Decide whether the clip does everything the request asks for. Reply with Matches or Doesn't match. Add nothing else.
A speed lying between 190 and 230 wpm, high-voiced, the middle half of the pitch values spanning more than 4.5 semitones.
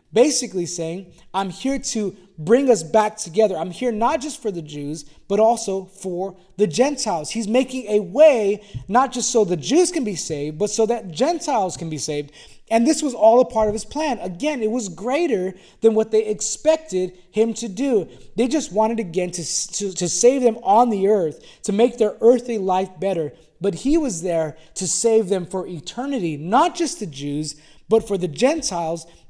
Matches